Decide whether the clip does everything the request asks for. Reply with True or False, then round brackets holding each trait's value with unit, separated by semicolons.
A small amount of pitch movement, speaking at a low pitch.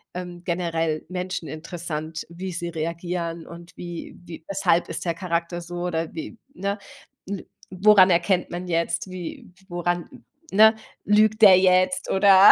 False (1.8 semitones; 175 Hz)